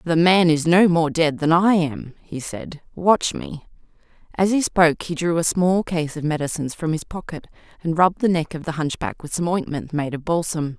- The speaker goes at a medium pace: No, fast, 215 wpm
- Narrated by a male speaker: No, female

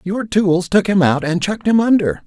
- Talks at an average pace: No, fast, 240 wpm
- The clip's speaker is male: Yes, male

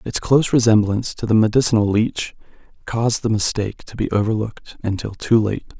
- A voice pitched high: No, low, 110 Hz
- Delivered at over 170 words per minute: No, average, 165 wpm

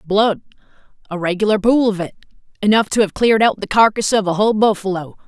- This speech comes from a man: No, female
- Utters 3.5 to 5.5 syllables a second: No, 6.0 syllables/s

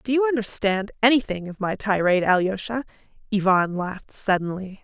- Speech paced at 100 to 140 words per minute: Yes, slow, 135 wpm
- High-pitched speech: Yes, high, 205 Hz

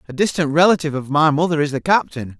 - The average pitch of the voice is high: No, medium, 155 Hz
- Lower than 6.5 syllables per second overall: No, 6.8 syllables/s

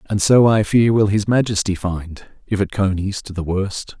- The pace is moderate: Yes, average, 195 wpm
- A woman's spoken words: No, male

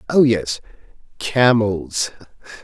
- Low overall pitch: Yes, low, 110 Hz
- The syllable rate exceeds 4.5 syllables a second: No, 2.9 syllables/s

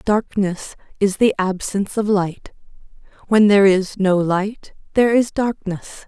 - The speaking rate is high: No, average, 140 wpm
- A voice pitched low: No, high, 200 Hz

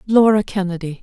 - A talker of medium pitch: No, high, 195 Hz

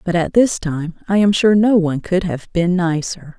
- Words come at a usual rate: No, fast, 230 wpm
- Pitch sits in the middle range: Yes, medium, 180 Hz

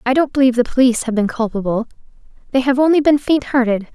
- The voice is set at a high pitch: Yes, very high, 250 Hz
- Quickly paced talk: Yes, fast, 215 wpm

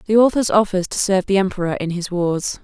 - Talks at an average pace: No, fast, 225 wpm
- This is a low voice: No, high, 190 Hz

